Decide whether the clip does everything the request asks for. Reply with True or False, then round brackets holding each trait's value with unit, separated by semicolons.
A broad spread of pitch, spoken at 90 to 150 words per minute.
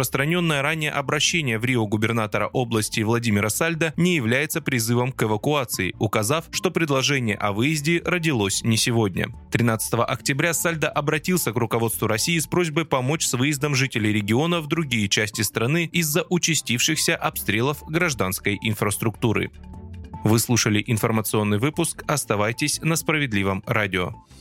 True (6.1 semitones; 130 wpm)